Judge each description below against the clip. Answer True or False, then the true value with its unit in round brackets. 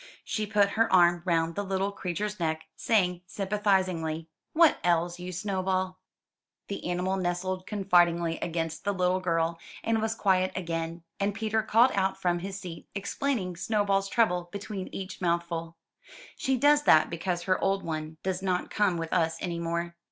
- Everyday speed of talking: True (160 wpm)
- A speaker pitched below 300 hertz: True (185 Hz)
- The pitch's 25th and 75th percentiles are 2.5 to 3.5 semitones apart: True (2.8 semitones)